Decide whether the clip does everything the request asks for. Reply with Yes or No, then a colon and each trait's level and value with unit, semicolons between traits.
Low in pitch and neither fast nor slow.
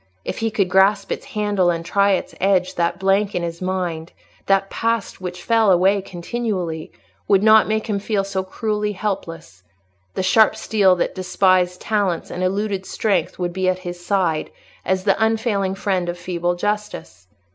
No: high, 190 Hz; average, 165 wpm